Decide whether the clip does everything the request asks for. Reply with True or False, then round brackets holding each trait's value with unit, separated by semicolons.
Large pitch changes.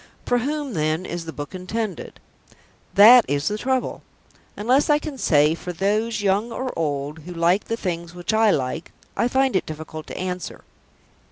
True (6.2 semitones)